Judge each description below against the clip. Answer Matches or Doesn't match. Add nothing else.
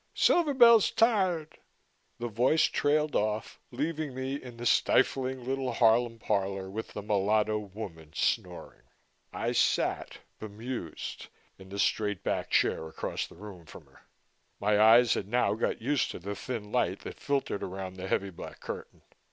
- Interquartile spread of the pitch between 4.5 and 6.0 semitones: Matches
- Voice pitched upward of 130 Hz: Doesn't match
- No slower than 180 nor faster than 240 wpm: Doesn't match